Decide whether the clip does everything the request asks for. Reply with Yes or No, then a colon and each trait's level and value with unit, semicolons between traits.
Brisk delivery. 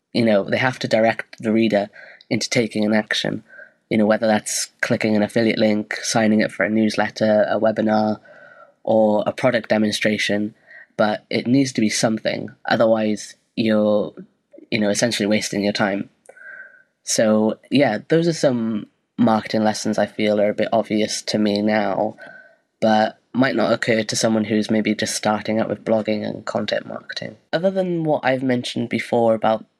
No: average, 170 wpm